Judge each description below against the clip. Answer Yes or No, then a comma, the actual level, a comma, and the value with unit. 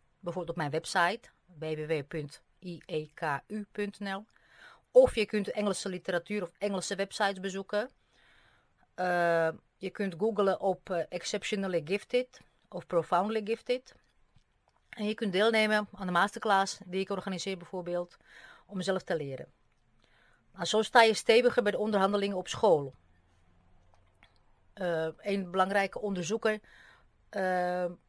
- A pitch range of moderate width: Yes, average, 3.5 semitones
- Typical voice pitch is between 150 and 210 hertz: Yes, high, 190 Hz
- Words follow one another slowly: Yes, slow, 115 wpm